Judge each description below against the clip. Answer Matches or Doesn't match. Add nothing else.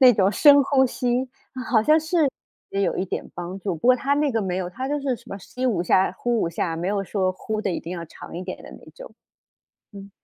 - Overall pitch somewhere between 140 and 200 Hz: Doesn't match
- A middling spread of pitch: Doesn't match